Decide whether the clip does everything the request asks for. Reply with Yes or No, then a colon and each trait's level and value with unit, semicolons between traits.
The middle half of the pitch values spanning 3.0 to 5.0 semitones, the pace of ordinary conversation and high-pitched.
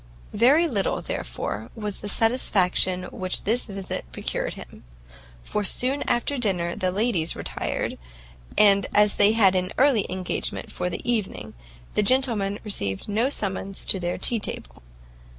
Yes: average, 3.9 semitones; average, 145 wpm; high, 205 Hz